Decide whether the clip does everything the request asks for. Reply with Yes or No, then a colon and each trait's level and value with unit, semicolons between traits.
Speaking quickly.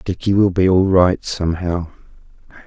No: slow, 135 wpm